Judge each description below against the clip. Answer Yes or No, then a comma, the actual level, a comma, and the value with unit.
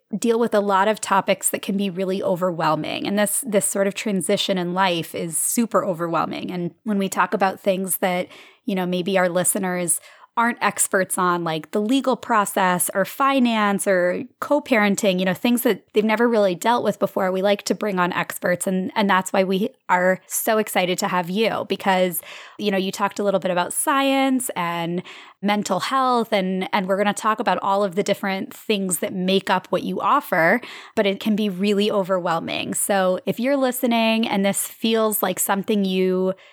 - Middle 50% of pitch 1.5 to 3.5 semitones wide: Yes, narrow, 2.6 semitones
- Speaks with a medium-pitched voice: No, high, 195 Hz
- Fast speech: No, average, 195 wpm